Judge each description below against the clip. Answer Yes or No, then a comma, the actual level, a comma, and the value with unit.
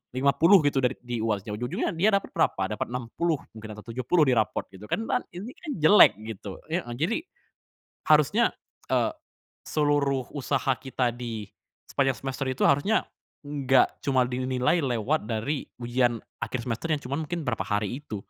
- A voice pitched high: No, low, 130 Hz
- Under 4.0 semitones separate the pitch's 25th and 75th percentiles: No, average, 4.3 semitones